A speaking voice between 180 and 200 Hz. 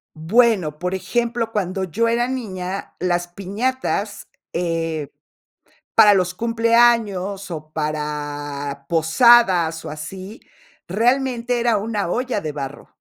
Yes: high, 190 Hz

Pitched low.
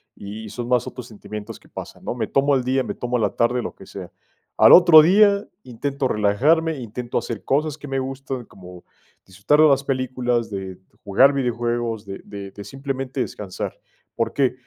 Yes: low, 125 Hz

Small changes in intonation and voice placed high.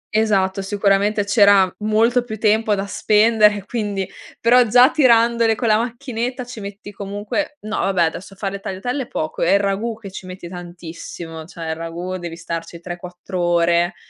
No: average, 3.8 semitones; high, 200 Hz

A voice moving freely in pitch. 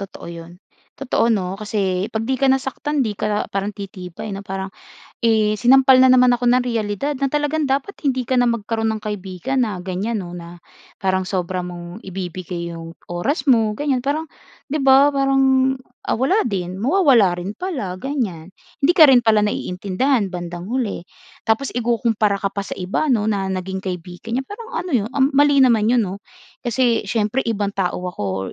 Yes: wide, 5.7 semitones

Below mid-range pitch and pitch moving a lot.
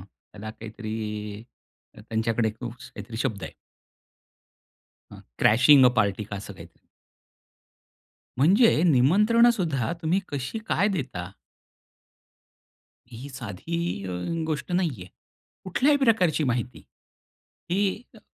Yes: low, 125 Hz; wide, 7.6 semitones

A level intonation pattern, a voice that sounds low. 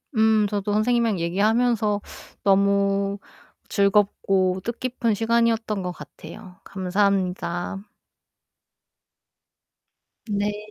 No: narrow, 2.2 semitones; high, 205 Hz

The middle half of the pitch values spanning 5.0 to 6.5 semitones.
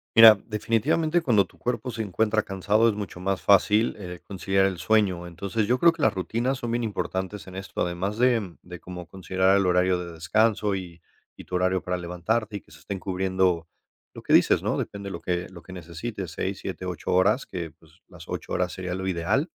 No: average, 3.3 semitones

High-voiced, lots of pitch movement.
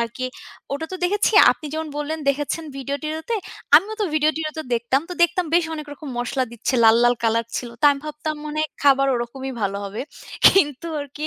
No: very high, 290 Hz; average, 3.6 semitones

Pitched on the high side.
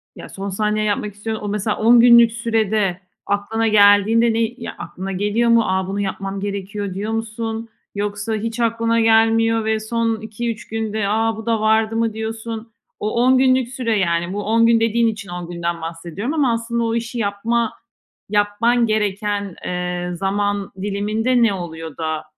Yes: high, 220 Hz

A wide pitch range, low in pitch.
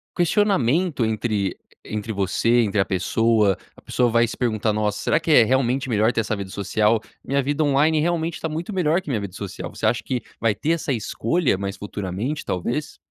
Yes: wide, 6.2 semitones; low, 115 Hz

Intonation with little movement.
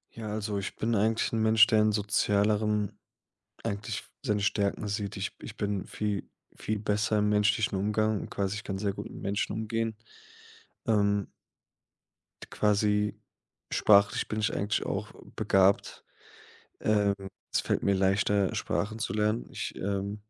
Yes: narrow, 1.1 semitones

